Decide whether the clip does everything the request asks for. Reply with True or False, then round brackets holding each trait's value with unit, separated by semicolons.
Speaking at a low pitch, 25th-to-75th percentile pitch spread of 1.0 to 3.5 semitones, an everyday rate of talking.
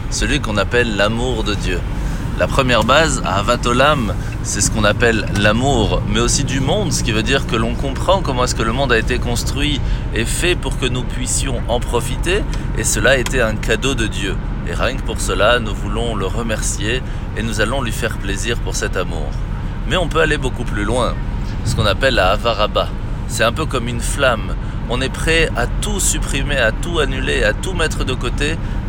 True (110 Hz; 2.6 semitones; 205 wpm)